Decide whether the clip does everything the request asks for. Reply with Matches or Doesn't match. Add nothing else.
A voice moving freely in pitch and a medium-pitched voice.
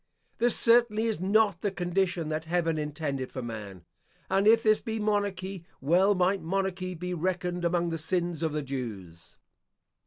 Doesn't match